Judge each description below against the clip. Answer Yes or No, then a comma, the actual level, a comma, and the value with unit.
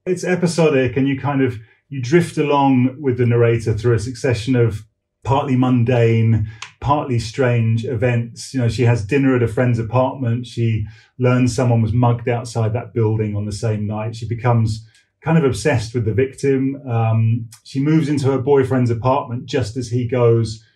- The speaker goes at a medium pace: Yes, average, 175 wpm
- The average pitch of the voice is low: Yes, low, 120 Hz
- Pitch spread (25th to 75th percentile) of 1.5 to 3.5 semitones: Yes, average, 2.7 semitones